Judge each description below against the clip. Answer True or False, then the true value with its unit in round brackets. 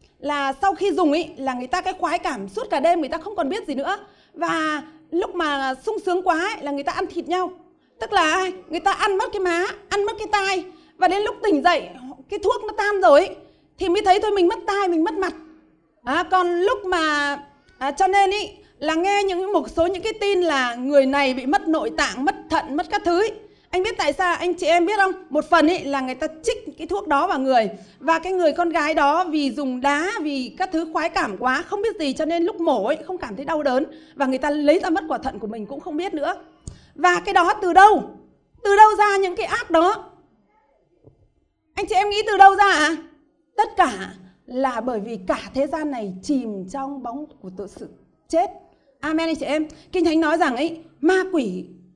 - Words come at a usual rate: True (240 wpm)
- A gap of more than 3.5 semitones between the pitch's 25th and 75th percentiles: True (4.7 semitones)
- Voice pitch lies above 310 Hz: True (335 Hz)